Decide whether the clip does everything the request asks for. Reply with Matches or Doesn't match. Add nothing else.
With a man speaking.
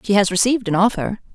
Doesn't match